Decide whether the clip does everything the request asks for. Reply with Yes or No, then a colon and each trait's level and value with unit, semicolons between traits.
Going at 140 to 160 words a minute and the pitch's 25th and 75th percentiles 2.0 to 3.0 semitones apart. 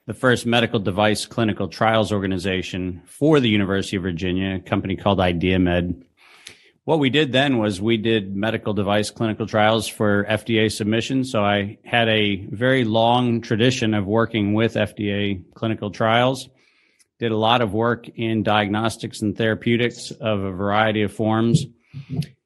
Yes: average, 150 wpm; narrow, 2.4 semitones